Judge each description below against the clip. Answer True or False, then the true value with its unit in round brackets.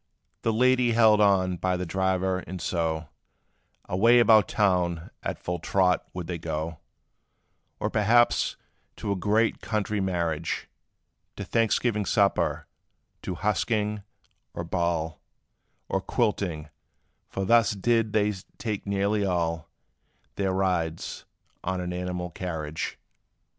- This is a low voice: True (95 Hz)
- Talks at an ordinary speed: False (120 wpm)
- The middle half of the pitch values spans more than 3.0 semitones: True (3.4 semitones)